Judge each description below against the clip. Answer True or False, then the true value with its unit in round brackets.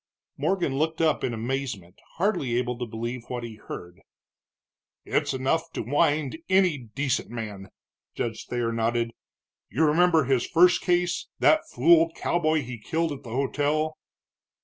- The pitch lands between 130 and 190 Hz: True (135 Hz)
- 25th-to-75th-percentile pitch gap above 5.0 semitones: True (5.4 semitones)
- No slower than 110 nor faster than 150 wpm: True (145 wpm)